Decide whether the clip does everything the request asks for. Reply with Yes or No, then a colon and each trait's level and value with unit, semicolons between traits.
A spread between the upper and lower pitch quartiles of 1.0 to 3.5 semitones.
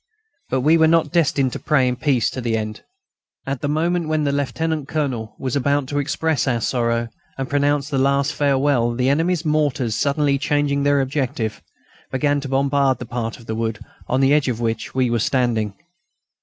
Yes: average, 3.1 semitones